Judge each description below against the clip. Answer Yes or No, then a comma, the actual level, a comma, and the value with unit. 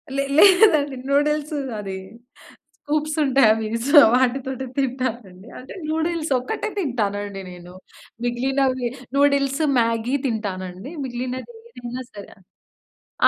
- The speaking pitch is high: Yes, very high, 260 Hz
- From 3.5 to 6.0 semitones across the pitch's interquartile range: Yes, average, 4.0 semitones